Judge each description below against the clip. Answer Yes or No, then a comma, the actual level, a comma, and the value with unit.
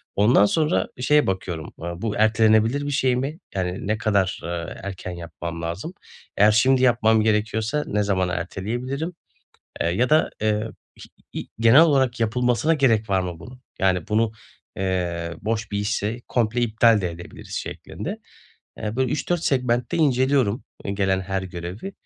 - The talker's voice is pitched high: No, low, 110 Hz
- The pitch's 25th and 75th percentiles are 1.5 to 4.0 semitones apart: No, average, 4.9 semitones